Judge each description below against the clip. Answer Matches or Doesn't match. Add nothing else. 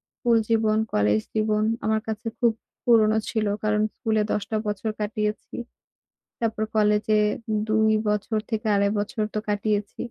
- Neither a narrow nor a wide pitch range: Doesn't match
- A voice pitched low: Doesn't match